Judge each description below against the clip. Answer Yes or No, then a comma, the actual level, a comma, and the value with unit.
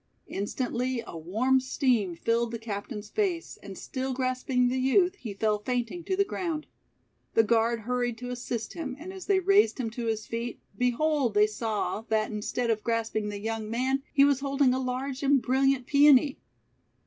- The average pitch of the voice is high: Yes, very high, 250 Hz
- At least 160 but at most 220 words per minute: Yes, average, 180 wpm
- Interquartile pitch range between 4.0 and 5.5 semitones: No, average, 3.4 semitones